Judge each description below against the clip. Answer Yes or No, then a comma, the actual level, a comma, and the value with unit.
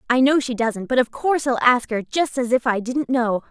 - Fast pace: Yes, fast, 275 wpm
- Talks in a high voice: Yes, very high, 250 Hz